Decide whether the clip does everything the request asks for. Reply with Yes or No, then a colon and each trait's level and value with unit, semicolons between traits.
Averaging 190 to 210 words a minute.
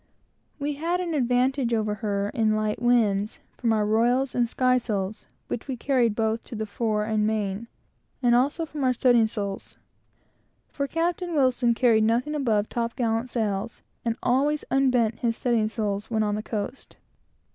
No: average, 165 wpm